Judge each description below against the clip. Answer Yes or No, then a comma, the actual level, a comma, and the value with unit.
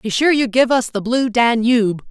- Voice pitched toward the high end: Yes, high, 235 Hz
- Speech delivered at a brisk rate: Yes, fast, 230 wpm